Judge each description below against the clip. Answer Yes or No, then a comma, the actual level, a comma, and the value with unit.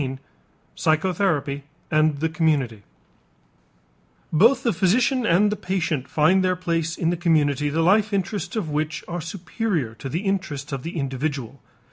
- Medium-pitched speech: Yes, medium, 165 Hz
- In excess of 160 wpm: No, average, 150 wpm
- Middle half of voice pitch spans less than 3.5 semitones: No, average, 4.5 semitones